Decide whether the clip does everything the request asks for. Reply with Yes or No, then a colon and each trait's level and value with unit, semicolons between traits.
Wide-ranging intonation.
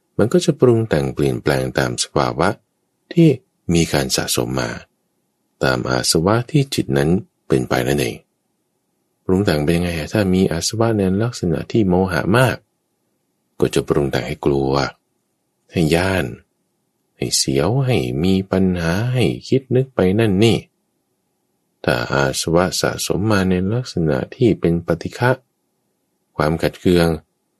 Yes: wide, 7.1 semitones